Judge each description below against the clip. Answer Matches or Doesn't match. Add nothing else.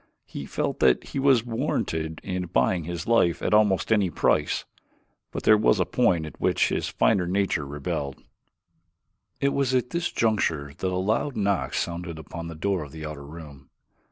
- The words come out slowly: Doesn't match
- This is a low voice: Matches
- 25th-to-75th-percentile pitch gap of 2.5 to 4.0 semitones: Doesn't match